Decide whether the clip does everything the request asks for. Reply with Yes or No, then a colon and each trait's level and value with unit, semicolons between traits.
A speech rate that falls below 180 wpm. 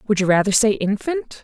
No: fast, 210 wpm